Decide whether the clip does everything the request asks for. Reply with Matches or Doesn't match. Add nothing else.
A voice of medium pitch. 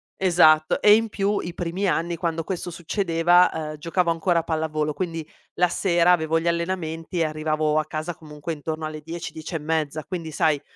Matches